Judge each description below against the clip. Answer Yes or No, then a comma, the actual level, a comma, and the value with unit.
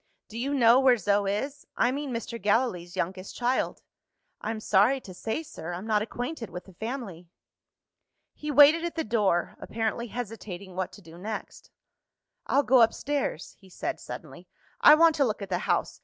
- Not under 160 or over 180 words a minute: Yes, average, 175 wpm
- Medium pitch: No, high, 225 Hz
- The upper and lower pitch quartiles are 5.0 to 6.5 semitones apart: Yes, wide, 5.5 semitones